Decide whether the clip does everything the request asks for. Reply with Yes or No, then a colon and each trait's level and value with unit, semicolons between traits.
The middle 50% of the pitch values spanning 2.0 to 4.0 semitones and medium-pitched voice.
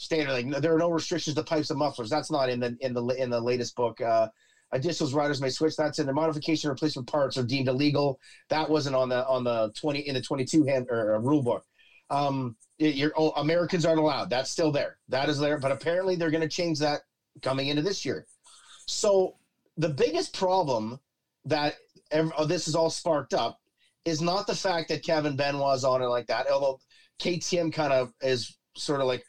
Yes: average, 3.5 semitones; medium, 150 Hz